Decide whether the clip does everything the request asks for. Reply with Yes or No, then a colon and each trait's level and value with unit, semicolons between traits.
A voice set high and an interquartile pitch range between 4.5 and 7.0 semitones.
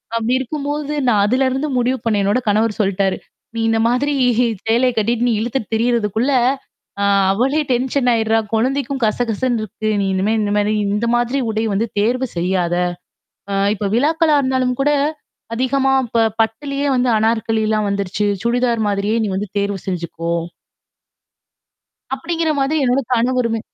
No: high, 230 Hz; average, 3.7 semitones